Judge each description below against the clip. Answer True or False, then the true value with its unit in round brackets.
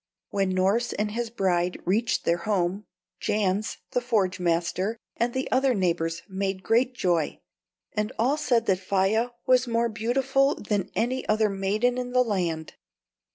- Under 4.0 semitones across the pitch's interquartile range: False (4.3 semitones)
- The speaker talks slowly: False (155 wpm)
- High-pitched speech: True (210 Hz)